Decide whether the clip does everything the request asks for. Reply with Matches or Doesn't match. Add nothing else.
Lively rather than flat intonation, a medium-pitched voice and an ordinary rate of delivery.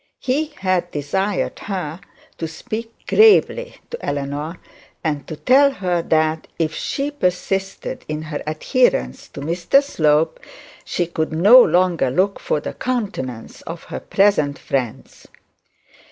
Doesn't match